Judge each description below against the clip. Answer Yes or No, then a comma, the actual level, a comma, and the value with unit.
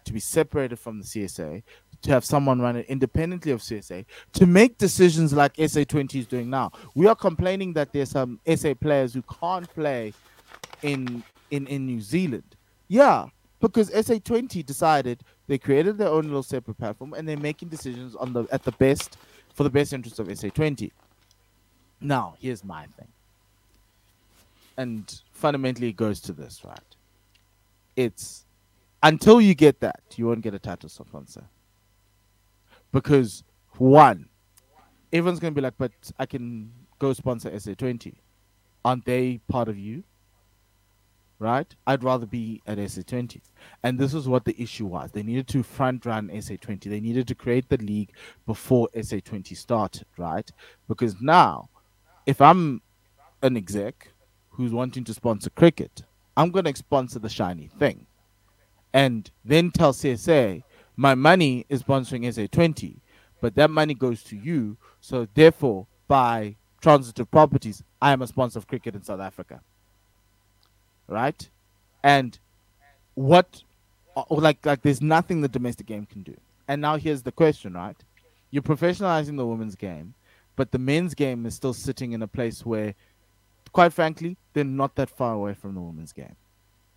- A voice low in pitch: Yes, low, 120 Hz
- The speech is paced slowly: No, average, 160 wpm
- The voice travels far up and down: Yes, wide, 5.9 semitones